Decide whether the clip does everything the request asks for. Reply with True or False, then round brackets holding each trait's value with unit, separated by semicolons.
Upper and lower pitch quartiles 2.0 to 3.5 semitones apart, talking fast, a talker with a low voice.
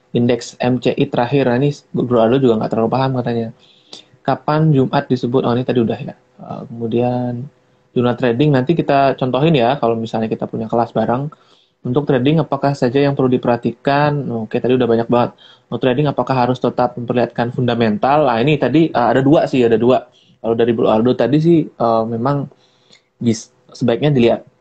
True (2.7 semitones; 170 wpm; 125 Hz)